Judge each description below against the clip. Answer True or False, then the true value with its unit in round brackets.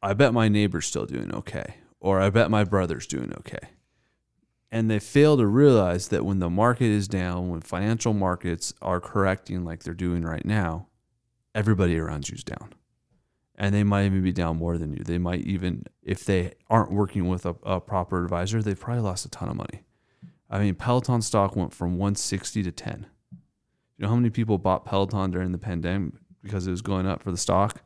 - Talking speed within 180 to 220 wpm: True (205 wpm)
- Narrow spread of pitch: False (3.5 semitones)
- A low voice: True (100 Hz)